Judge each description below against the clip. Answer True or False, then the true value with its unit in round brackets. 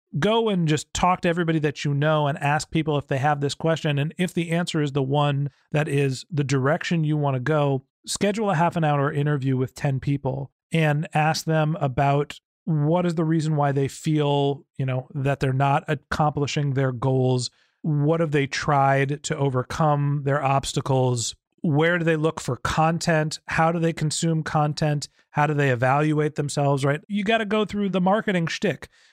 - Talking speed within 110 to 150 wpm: False (190 wpm)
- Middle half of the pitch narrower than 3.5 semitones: True (2.6 semitones)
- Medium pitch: True (150 Hz)